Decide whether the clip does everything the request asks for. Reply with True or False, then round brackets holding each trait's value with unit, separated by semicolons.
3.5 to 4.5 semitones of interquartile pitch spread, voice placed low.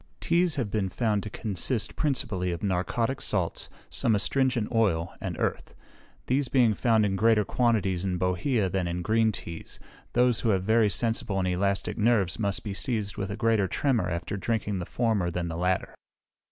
True (3.8 semitones; 105 Hz)